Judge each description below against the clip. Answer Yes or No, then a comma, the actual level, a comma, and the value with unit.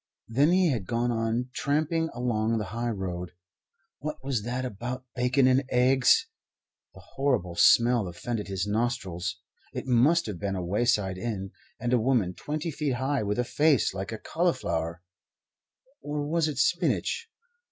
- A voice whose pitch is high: No, low, 120 Hz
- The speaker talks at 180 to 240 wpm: No, average, 155 wpm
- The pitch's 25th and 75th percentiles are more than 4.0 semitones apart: Yes, average, 5.2 semitones